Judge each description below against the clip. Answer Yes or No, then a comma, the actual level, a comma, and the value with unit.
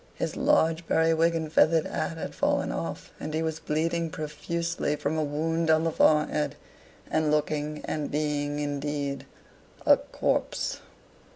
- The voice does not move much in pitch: Yes, narrow, 1.6 semitones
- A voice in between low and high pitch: Yes, medium, 155 Hz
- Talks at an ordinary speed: Yes, average, 145 wpm